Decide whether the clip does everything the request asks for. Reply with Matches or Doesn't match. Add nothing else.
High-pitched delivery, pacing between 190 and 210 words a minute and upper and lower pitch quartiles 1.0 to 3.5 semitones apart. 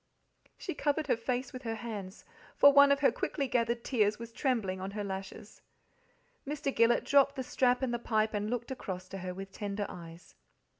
Doesn't match